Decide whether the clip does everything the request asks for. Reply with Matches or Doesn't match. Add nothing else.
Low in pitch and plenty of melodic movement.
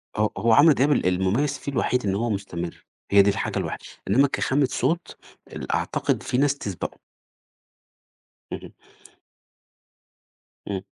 Matches